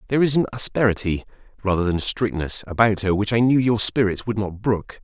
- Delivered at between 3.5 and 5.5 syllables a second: No, 5.8 syllables/s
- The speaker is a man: Yes, male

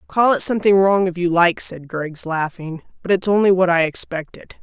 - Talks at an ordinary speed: No, fast, 210 wpm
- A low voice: No, medium, 180 Hz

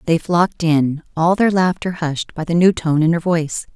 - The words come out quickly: Yes, fast, 225 wpm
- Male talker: No, female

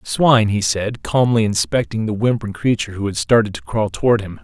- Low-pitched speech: Yes, low, 110 Hz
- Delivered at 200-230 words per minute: Yes, fast, 205 wpm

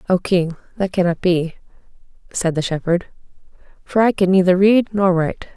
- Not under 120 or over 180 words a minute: Yes, average, 160 wpm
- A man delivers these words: No, female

